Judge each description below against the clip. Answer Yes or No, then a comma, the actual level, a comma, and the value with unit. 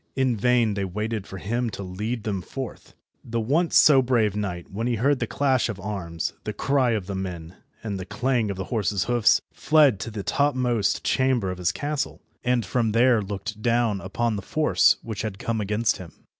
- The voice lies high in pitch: No, low, 110 Hz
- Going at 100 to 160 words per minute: No, average, 200 wpm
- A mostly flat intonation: No, average, 3.8 semitones